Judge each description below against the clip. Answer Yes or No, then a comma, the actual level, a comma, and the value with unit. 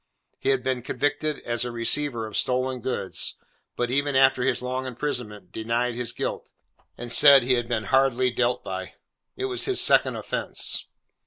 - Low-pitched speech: Yes, low, 125 Hz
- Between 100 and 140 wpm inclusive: No, average, 170 wpm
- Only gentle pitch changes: Yes, narrow, 2.2 semitones